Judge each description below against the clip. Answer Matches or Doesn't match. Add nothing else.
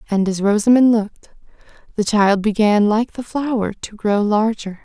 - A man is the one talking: Doesn't match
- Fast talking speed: Doesn't match